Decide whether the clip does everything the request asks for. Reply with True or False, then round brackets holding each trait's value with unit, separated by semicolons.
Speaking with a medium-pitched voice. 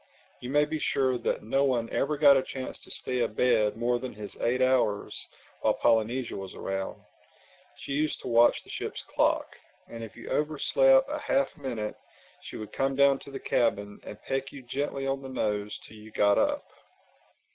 False (125 Hz)